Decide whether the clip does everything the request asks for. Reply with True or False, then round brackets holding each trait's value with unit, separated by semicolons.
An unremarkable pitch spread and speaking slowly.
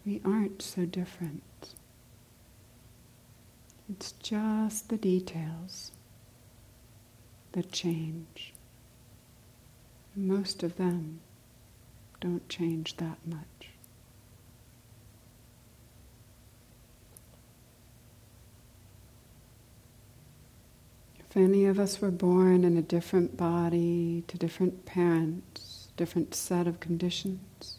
False (7.1 semitones; 75 wpm)